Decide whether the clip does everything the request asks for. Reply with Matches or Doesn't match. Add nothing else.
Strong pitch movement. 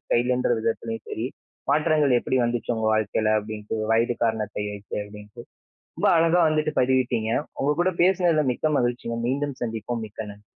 Doesn't match